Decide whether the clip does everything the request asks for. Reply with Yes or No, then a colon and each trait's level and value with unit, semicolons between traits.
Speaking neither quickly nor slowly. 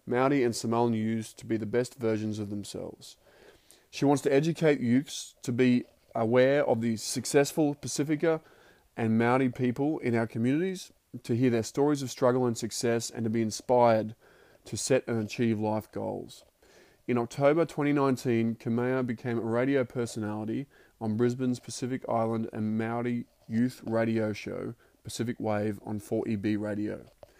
Yes: average, 150 wpm